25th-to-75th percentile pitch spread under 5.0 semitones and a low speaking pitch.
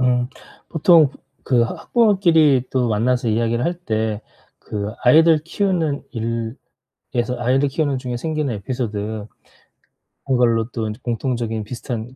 Yes: average, 4.3 semitones; low, 125 Hz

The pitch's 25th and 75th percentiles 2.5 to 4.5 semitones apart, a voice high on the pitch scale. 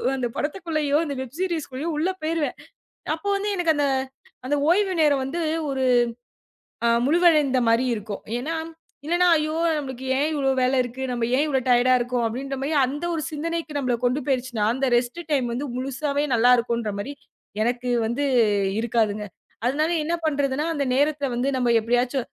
Yes: average, 3.8 semitones; very high, 275 Hz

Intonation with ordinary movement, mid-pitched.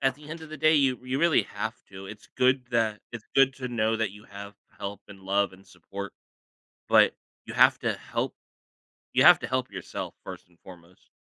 No: average, 4.7 semitones; low, 110 Hz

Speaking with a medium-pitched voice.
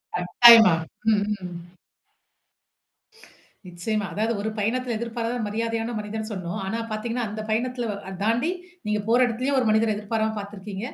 No: high, 220 Hz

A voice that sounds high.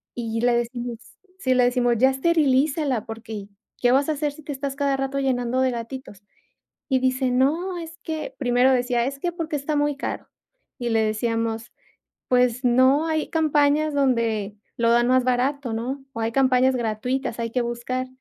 Yes: very high, 255 Hz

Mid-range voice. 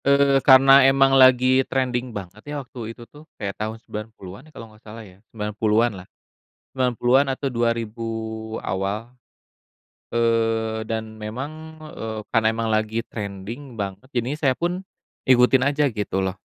No: low, 115 Hz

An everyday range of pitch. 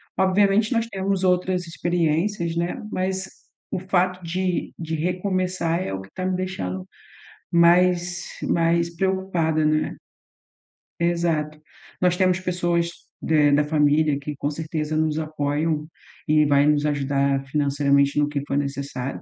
Yes: average, 3.6 semitones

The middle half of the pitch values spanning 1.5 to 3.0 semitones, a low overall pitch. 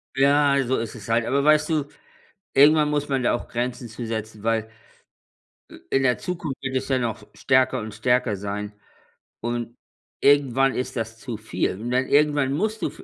No: average, 3.8 semitones; low, 125 Hz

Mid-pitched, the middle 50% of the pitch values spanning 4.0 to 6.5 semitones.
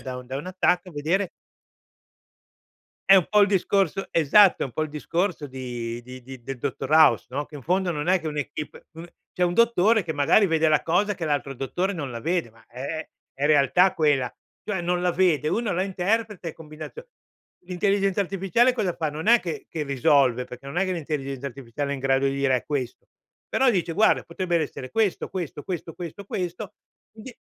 Yes: medium, 165 Hz; wide, 5.4 semitones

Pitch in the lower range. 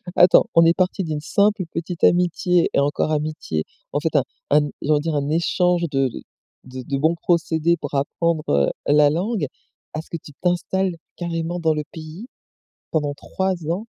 No: medium, 165 Hz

